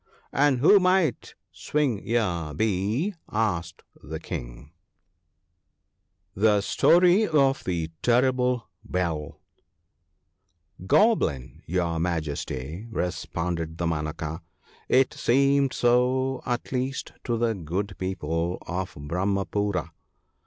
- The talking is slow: Yes, slow, 105 wpm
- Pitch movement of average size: No, wide, 7.5 semitones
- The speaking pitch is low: Yes, low, 100 Hz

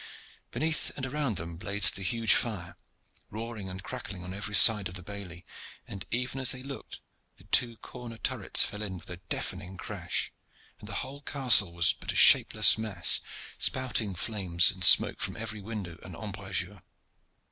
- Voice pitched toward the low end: Yes, low, 105 Hz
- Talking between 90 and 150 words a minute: No, average, 170 wpm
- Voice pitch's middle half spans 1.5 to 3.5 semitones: No, average, 3.9 semitones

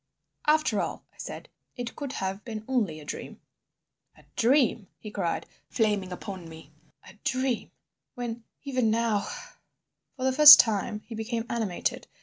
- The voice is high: Yes, high, 225 Hz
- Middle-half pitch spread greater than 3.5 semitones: Yes, average, 4.2 semitones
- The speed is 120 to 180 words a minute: Yes, average, 140 wpm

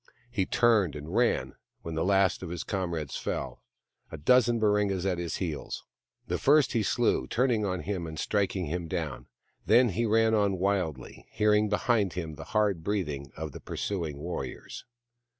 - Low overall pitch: Yes, very low, 95 Hz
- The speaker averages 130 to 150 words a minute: No, average, 170 wpm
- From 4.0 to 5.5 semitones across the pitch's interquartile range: Yes, average, 4.4 semitones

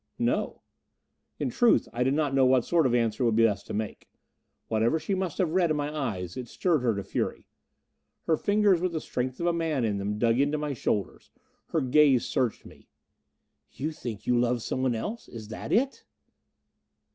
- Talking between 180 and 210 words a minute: Yes, average, 200 wpm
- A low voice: Yes, low, 130 Hz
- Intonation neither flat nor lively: No, wide, 5.7 semitones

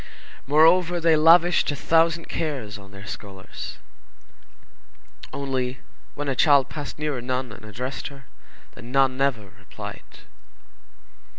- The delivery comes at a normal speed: No, slow, 125 wpm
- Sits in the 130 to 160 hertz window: Yes, low, 135 Hz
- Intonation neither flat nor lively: Yes, average, 4.4 semitones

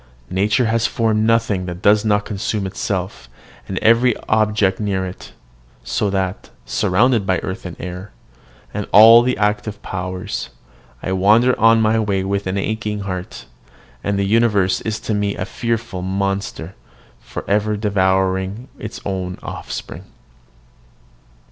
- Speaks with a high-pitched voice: No, low, 100 Hz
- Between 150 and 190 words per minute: No, slow, 135 wpm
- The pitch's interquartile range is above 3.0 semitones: No, narrow, 2.6 semitones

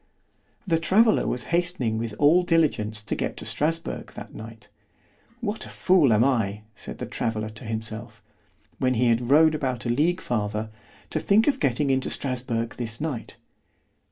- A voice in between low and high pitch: No, low, 125 Hz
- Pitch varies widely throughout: Yes, wide, 6.5 semitones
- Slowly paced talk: No, average, 165 wpm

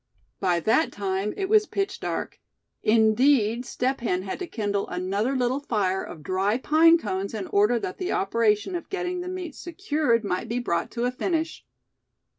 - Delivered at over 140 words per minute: Yes, average, 175 wpm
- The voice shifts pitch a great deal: Yes, wide, 7.9 semitones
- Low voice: No, high, 235 Hz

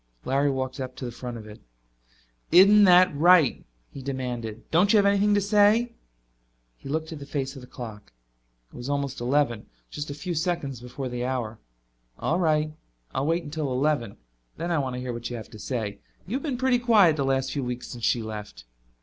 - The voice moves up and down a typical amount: No, wide, 5.9 semitones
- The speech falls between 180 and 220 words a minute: Yes, average, 200 wpm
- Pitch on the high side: No, medium, 140 Hz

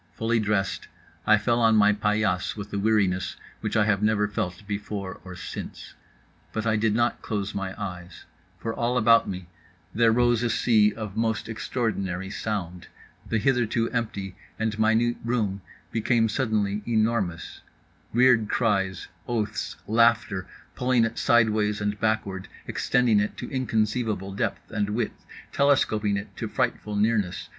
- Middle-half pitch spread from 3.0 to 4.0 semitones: No, narrow, 2.4 semitones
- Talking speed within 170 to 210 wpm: No, average, 145 wpm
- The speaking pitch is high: No, low, 110 Hz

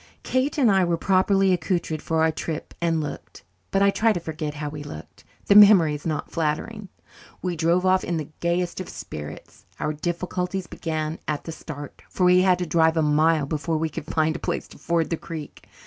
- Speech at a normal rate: No, fast, 210 wpm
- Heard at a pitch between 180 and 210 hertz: No, medium, 165 Hz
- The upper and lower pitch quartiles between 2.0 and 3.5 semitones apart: Yes, average, 2.9 semitones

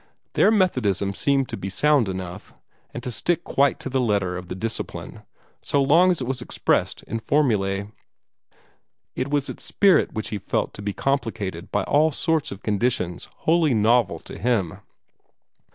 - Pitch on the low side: Yes, low, 120 Hz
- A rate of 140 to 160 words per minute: No, average, 170 wpm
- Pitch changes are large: Yes, wide, 6.3 semitones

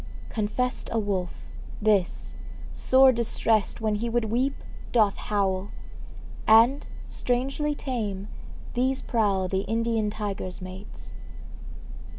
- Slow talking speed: Yes, slow, 105 wpm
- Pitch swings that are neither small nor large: Yes, average, 3.4 semitones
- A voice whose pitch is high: Yes, high, 220 Hz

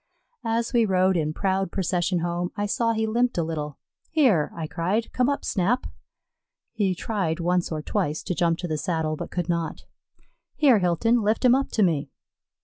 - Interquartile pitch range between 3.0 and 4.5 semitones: No, average, 5.1 semitones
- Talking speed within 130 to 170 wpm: No, average, 185 wpm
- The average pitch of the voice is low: No, medium, 185 Hz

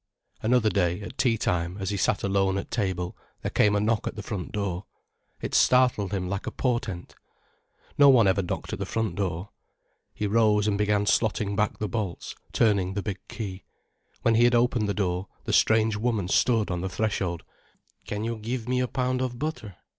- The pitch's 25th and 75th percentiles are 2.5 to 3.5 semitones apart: Yes, average, 3.0 semitones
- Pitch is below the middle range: Yes, low, 105 Hz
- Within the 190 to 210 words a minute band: Yes, average, 200 wpm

